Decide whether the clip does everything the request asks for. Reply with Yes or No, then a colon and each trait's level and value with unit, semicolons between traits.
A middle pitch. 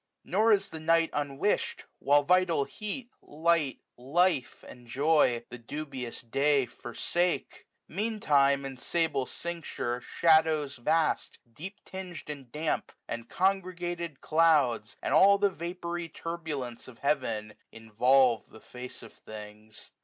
Yes: medium, 150 Hz